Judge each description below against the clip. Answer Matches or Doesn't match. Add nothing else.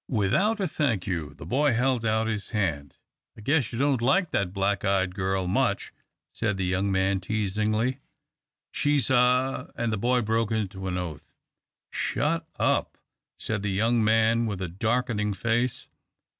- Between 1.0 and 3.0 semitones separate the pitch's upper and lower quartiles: Doesn't match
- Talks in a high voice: Doesn't match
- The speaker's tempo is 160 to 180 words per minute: Matches